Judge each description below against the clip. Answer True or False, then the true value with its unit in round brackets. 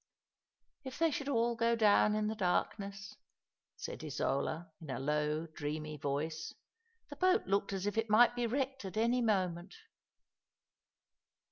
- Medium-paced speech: True (160 wpm)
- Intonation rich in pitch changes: True (6.9 semitones)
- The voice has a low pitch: False (205 Hz)